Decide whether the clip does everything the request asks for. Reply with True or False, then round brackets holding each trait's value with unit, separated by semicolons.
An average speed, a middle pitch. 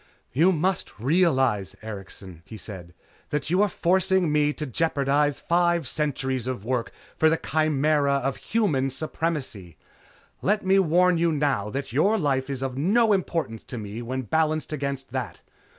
True (155 wpm; 145 Hz)